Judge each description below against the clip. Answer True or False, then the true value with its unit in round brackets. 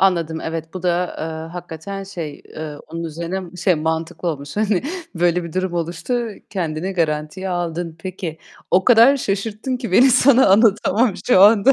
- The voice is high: False (180 Hz)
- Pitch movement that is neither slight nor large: True (3.4 semitones)